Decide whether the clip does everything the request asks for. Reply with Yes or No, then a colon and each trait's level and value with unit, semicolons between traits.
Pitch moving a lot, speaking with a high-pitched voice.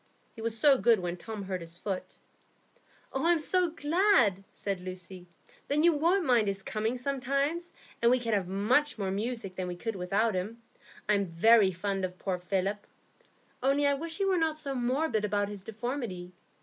Yes: wide, 6.5 semitones; high, 225 Hz